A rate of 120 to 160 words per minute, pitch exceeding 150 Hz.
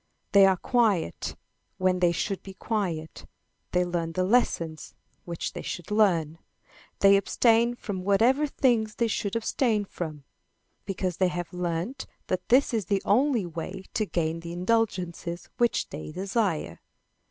Yes: average, 145 wpm; high, 190 Hz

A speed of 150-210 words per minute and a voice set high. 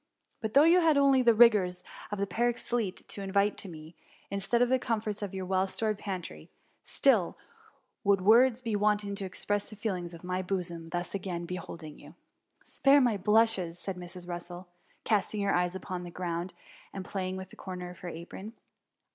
Yes: average, 200 wpm; high, 195 Hz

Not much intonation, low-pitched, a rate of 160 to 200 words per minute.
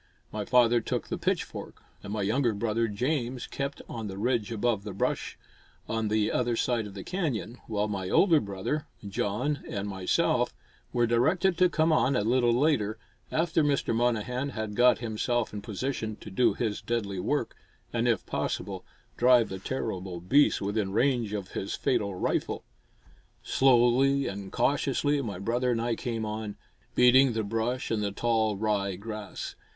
No: average, 3.5 semitones; low, 115 Hz; average, 165 wpm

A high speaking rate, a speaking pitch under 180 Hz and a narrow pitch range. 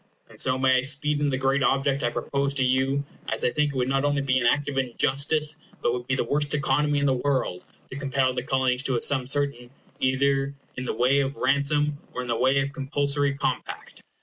Yes: fast, 230 wpm; low, 135 Hz; narrow, 1.5 semitones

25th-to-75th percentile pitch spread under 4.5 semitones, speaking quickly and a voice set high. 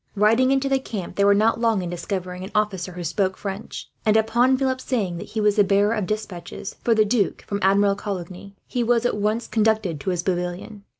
Yes: average, 3.0 semitones; fast, 220 wpm; high, 205 Hz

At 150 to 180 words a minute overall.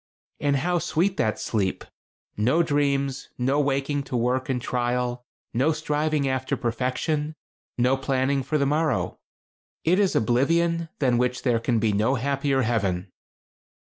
No: average, 140 wpm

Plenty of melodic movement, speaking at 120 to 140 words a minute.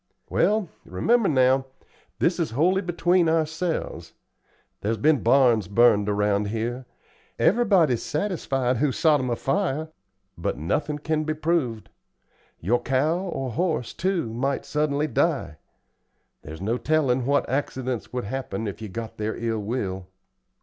Yes: wide, 5.8 semitones; slow, 135 wpm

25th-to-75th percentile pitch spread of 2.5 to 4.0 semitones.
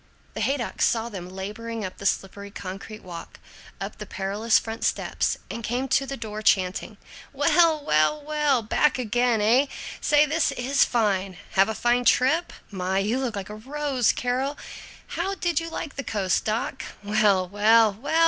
No: average, 5.3 semitones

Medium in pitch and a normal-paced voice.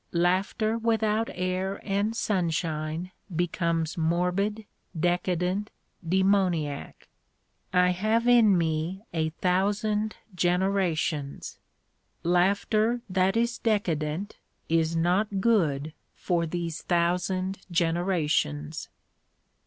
No: medium, 180 Hz; slow, 80 wpm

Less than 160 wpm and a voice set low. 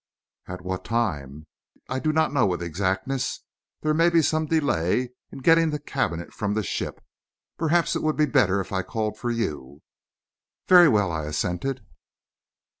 No: average, 165 wpm; low, 115 Hz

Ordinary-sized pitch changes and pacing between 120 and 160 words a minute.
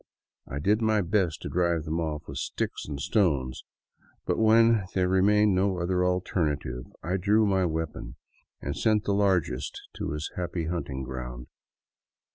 Yes: average, 5.0 semitones; average, 155 wpm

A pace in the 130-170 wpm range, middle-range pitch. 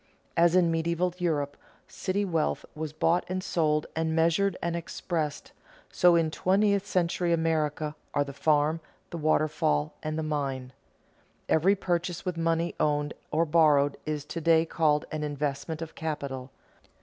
Yes: average, 150 wpm; medium, 160 Hz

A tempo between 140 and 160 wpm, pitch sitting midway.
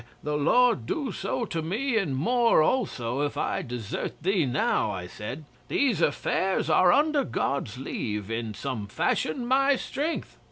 Yes: average, 155 wpm; medium, 155 Hz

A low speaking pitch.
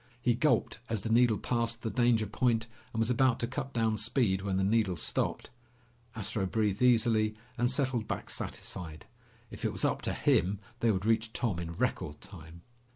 Yes: low, 110 Hz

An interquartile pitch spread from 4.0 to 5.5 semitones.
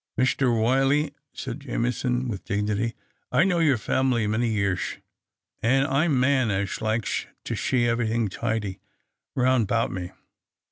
No: average, 3.3 semitones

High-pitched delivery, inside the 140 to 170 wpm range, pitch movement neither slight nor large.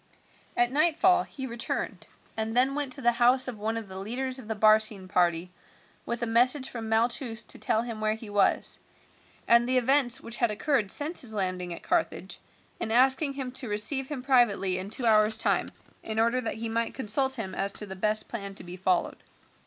No: high, 230 Hz; fast, 205 wpm; average, 3.4 semitones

